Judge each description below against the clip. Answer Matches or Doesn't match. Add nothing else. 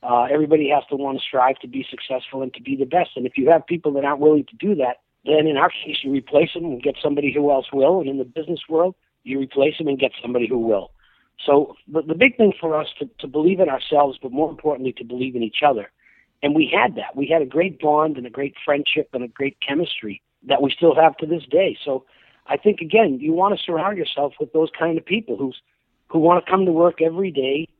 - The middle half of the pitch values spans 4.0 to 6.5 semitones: Doesn't match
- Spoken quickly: Matches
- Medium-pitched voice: Matches